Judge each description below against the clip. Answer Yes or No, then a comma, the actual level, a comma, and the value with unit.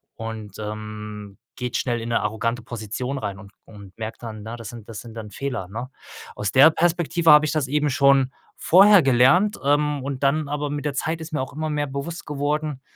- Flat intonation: No, average, 5.0 semitones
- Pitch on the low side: Yes, low, 130 Hz